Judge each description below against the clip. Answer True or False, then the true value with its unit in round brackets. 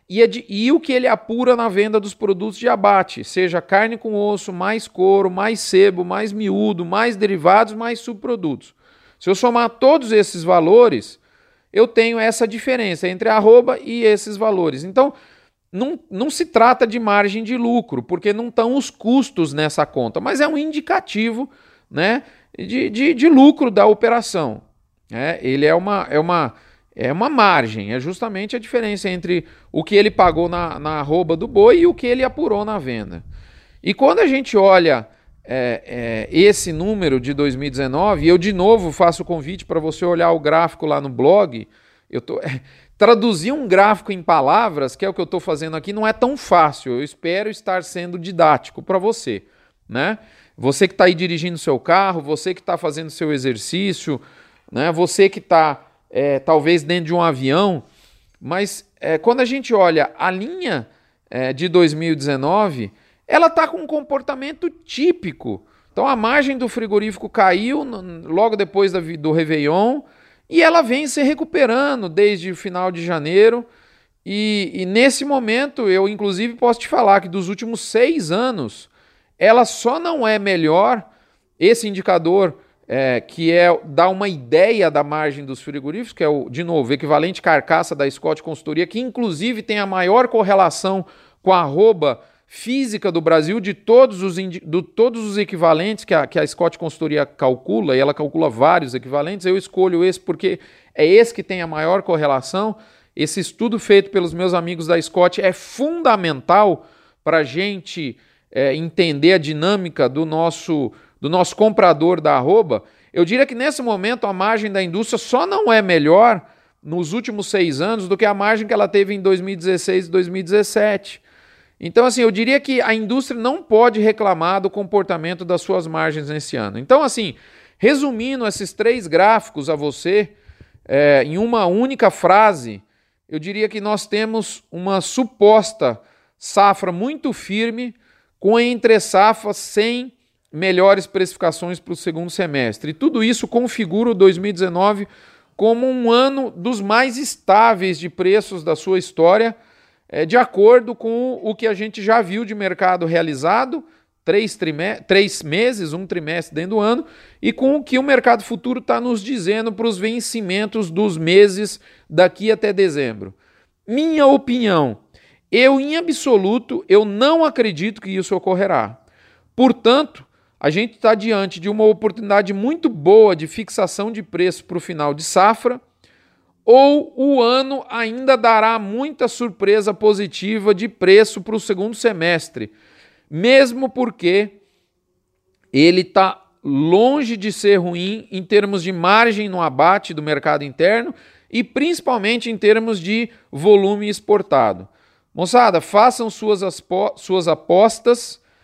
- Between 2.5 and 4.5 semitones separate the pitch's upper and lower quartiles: False (5.3 semitones)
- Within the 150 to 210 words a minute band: True (160 wpm)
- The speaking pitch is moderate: False (200 Hz)